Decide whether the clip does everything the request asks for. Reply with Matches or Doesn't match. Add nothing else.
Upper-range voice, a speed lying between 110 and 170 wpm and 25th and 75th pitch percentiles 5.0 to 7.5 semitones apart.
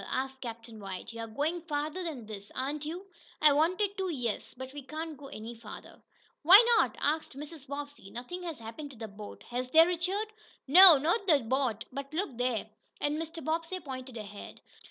Doesn't match